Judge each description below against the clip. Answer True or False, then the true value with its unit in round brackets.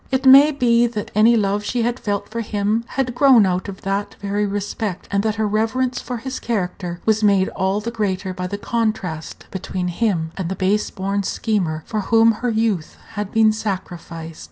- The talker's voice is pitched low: False (210 Hz)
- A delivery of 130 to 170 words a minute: False (195 wpm)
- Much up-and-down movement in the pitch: False (3.2 semitones)